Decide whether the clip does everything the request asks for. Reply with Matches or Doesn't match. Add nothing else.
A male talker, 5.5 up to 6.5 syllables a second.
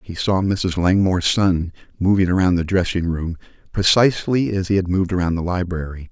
Matches